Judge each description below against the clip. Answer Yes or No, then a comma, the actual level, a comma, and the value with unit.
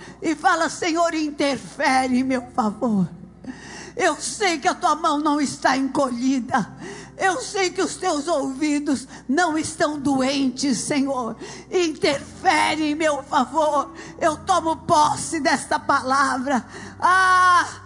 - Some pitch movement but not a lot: Yes, average, 4.0 semitones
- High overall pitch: Yes, very high, 295 Hz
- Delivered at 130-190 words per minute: No, slow, 120 wpm